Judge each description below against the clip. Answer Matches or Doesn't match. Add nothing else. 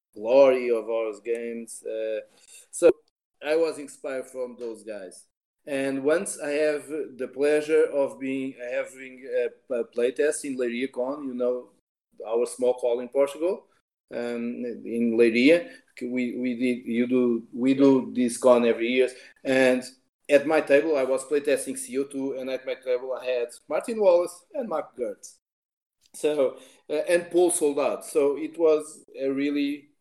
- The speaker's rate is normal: Matches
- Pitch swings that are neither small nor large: Matches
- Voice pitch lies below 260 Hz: Matches